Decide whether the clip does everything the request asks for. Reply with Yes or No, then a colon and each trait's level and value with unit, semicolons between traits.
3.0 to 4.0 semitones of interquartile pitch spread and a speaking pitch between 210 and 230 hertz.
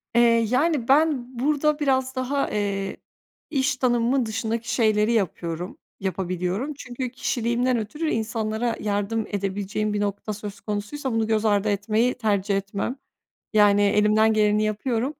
Yes: average, 3.5 semitones; high, 220 Hz